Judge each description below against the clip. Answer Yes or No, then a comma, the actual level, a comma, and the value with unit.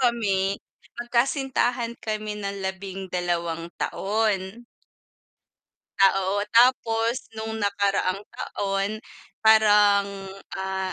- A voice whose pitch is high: Yes, high, 205 Hz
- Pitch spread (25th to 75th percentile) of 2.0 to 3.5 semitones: Yes, average, 2.8 semitones